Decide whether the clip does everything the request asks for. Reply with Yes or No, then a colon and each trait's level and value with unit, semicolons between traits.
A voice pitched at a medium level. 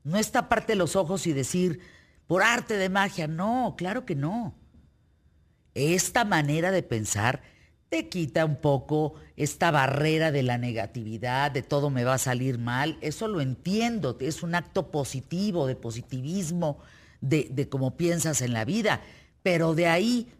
Yes: medium, 160 Hz